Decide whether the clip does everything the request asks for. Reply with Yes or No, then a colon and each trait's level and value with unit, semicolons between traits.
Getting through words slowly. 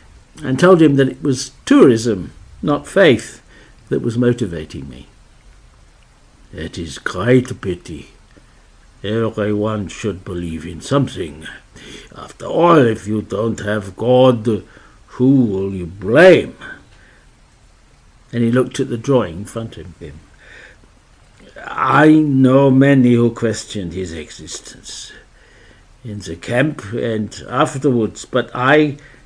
Yes: slow, 120 wpm